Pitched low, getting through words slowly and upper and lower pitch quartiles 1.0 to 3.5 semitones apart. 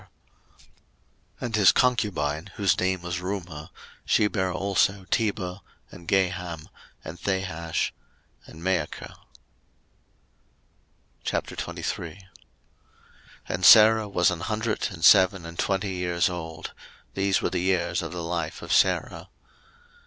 Yes: very low, 95 Hz; slow, 115 wpm; narrow, 2.5 semitones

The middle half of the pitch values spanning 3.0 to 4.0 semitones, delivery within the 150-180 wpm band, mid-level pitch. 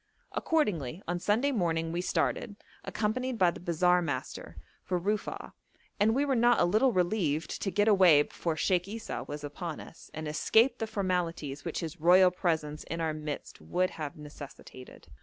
No: average, 5.1 semitones; average, 170 wpm; medium, 175 Hz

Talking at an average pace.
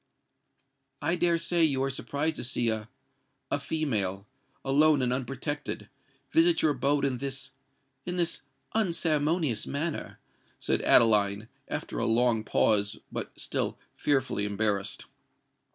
No: slow, 110 wpm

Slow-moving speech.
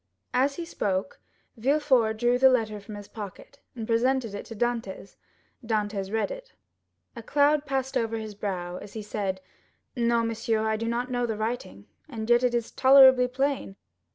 No: average, 175 wpm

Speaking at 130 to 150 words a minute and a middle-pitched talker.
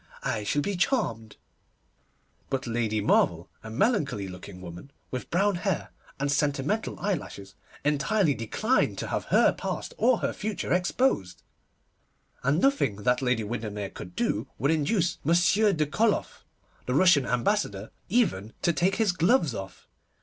Yes: average, 140 wpm; medium, 145 Hz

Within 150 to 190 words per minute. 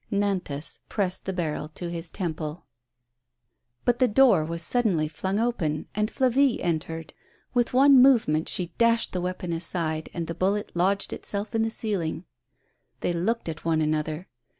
Yes: average, 155 wpm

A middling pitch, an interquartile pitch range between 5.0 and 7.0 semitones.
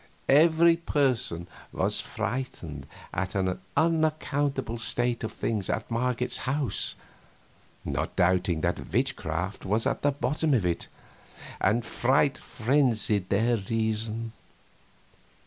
No: low, 115 Hz; wide, 5.5 semitones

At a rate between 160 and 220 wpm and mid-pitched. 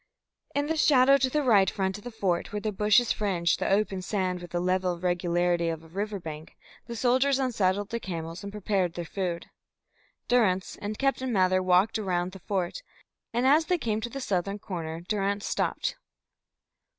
No: average, 185 wpm; high, 195 Hz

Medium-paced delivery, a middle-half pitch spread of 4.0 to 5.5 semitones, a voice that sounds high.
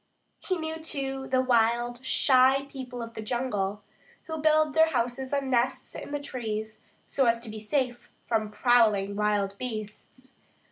No: average, 155 wpm; average, 3.6 semitones; high, 245 Hz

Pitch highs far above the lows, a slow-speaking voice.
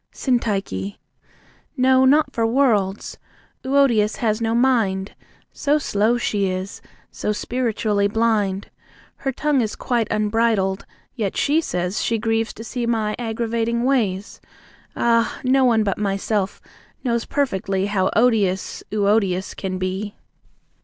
No: average, 3.3 semitones; slow, 125 wpm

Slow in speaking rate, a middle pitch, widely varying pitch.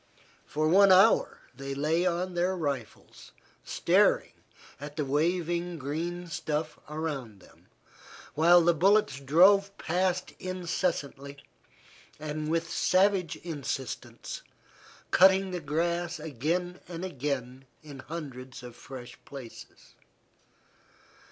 No: slow, 100 wpm; medium, 160 Hz; average, 4.1 semitones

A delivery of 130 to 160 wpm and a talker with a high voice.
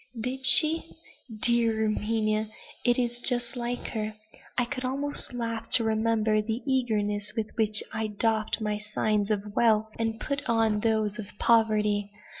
Yes: average, 150 wpm; high, 220 Hz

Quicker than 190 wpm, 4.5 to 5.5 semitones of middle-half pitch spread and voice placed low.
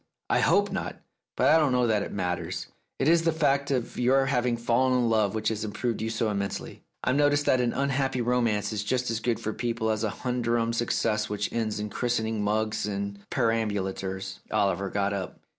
No: average, 200 wpm; average, 3.2 semitones; low, 115 Hz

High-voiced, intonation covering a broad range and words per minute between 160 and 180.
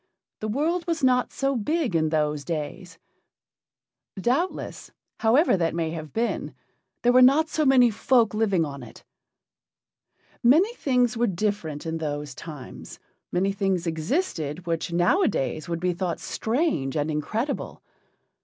No: high, 195 Hz; wide, 8.0 semitones; slow, 135 wpm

